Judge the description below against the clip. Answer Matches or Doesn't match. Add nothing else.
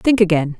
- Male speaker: Doesn't match